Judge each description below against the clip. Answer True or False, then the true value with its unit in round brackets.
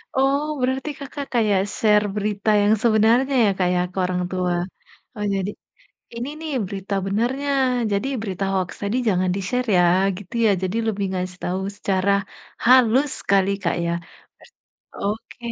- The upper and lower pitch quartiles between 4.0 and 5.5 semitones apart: True (4.3 semitones)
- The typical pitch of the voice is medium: False (205 Hz)